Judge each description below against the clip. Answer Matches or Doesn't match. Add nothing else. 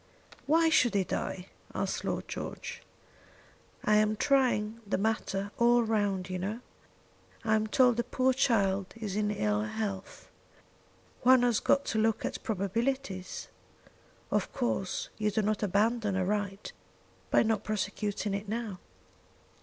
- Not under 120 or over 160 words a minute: Matches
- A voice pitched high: Matches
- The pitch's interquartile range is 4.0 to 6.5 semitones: Doesn't match